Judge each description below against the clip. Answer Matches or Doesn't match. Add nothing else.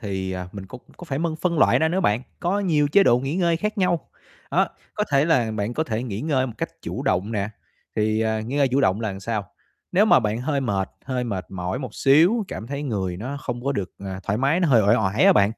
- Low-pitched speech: Matches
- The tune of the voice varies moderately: Doesn't match